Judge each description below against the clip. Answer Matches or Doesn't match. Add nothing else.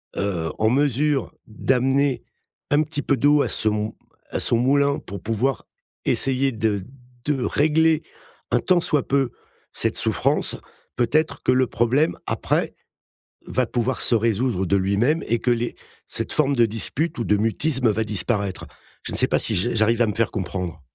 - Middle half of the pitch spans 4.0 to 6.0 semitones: Matches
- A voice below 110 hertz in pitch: Doesn't match